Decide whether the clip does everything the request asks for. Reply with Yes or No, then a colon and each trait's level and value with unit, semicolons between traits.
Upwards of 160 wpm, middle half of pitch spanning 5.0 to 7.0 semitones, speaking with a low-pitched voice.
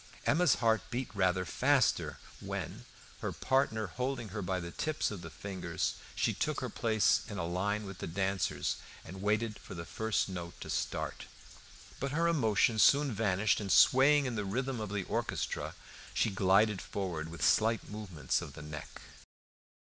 No: average, 170 wpm; average, 3.9 semitones; low, 105 Hz